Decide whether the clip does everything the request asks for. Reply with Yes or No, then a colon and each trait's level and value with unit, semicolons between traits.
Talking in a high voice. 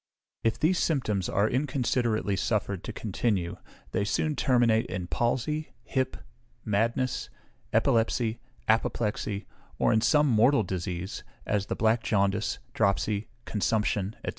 No: low, 110 Hz